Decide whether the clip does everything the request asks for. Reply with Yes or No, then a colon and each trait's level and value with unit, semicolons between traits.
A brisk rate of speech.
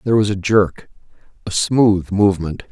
No: slow, 135 wpm